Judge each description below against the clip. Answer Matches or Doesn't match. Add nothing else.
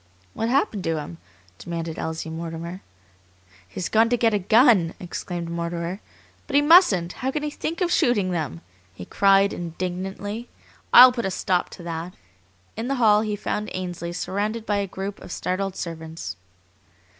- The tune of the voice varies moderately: Matches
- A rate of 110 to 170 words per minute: Matches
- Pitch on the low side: Doesn't match